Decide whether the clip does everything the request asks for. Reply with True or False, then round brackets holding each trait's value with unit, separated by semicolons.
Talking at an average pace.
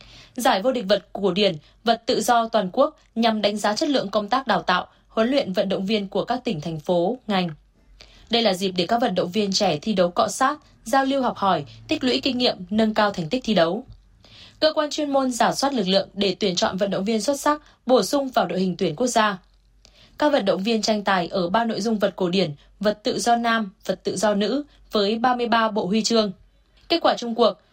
True (240 wpm)